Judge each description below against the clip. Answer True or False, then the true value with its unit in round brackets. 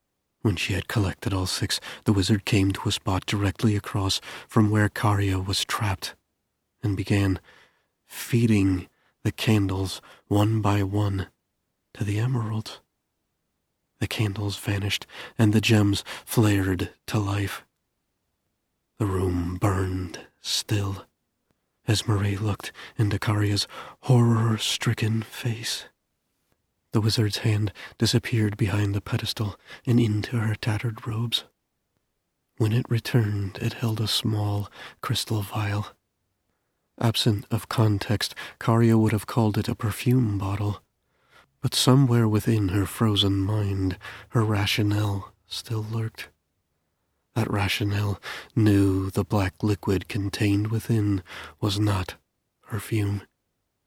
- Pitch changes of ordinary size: False (2.3 semitones)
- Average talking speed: False (115 wpm)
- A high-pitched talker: False (105 Hz)